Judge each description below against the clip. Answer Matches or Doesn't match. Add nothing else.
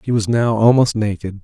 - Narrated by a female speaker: Doesn't match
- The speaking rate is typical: Doesn't match